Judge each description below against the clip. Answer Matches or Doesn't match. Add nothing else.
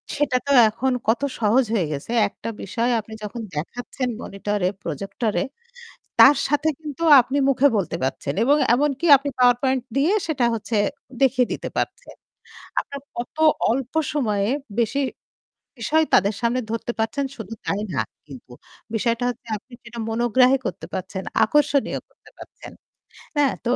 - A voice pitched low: Doesn't match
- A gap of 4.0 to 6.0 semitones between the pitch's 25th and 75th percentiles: Matches